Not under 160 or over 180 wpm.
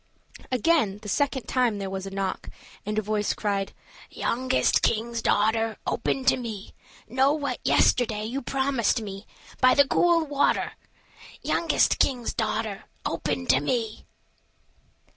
No: average, 140 wpm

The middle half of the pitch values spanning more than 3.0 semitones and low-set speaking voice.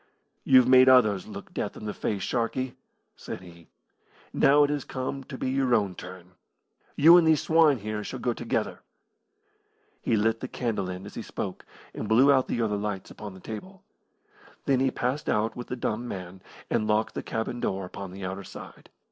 Yes: average, 4.7 semitones; low, 115 Hz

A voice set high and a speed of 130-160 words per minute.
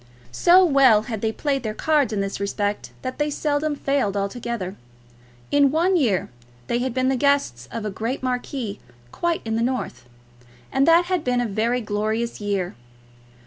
No: high, 245 Hz; average, 175 wpm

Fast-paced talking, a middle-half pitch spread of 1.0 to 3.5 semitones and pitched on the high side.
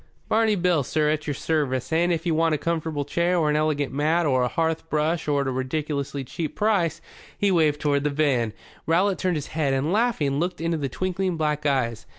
No: fast, 210 wpm; average, 2.9 semitones; medium, 155 Hz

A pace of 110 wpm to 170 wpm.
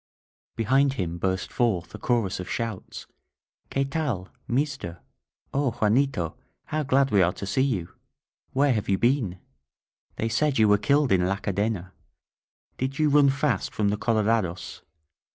Yes: average, 150 wpm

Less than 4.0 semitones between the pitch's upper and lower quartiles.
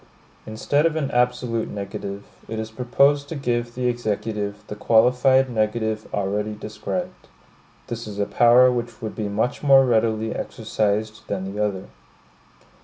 Yes: average, 2.9 semitones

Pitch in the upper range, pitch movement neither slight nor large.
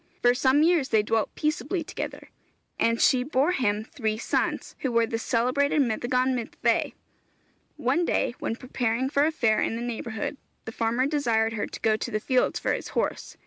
Yes: high, 245 Hz; average, 3.7 semitones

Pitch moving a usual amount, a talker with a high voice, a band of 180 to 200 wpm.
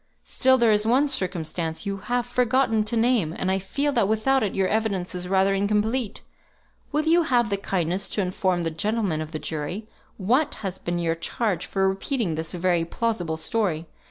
Yes: average, 4.8 semitones; high, 200 Hz; average, 185 wpm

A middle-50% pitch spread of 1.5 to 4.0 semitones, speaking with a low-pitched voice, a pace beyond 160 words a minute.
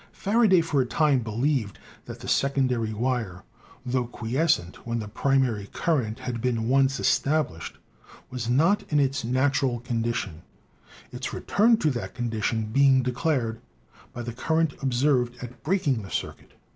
No: average, 3.5 semitones; low, 125 Hz; average, 145 wpm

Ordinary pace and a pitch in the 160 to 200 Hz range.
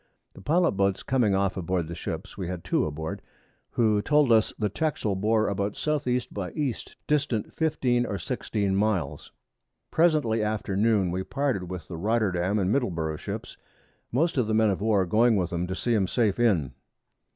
No: average, 180 wpm; low, 105 Hz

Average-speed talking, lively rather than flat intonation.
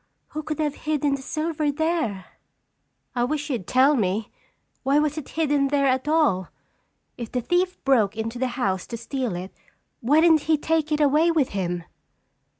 No: average, 175 wpm; average, 4.7 semitones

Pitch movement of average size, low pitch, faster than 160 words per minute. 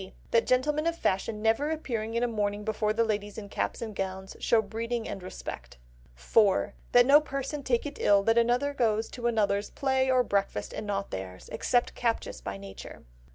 No: average, 3.6 semitones; high, 225 Hz; average, 190 wpm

